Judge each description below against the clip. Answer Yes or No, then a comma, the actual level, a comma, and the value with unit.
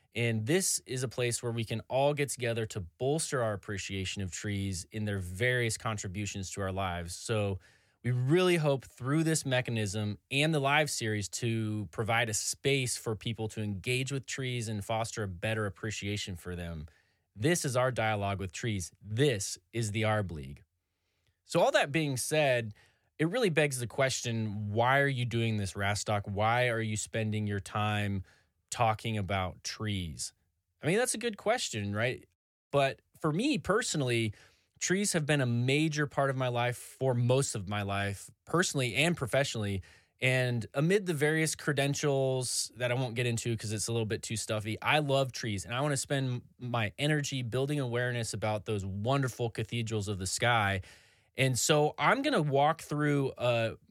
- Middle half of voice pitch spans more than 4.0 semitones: Yes, average, 4.6 semitones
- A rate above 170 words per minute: Yes, average, 180 wpm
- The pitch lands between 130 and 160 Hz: No, low, 115 Hz